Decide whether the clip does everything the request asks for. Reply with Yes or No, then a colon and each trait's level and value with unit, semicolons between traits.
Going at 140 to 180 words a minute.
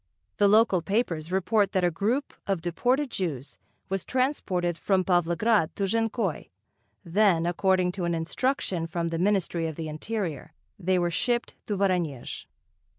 Yes: average, 150 wpm